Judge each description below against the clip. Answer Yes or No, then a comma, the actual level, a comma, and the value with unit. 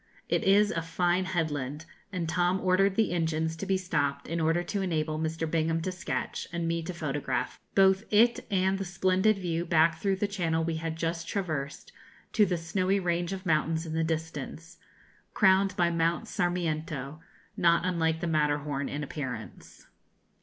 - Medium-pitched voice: Yes, medium, 170 Hz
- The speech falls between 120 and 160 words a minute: No, average, 170 wpm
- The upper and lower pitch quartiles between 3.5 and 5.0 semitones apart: No, average, 2.7 semitones